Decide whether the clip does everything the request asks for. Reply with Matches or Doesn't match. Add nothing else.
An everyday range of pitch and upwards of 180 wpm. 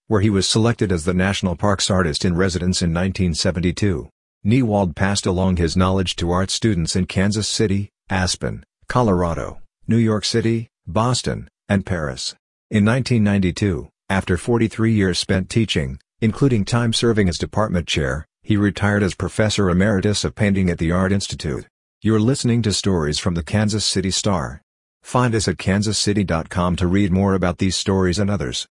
Doesn't match